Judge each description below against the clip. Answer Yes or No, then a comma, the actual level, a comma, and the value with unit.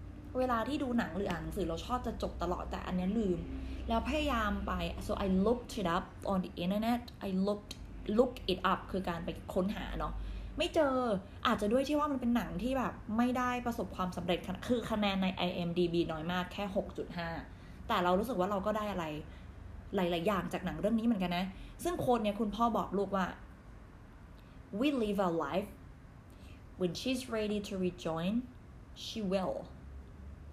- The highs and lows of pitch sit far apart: No, average, 4.6 semitones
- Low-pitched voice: No, high, 195 Hz